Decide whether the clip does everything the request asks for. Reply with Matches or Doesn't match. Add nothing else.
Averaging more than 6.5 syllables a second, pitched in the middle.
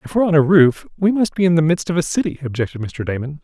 Matches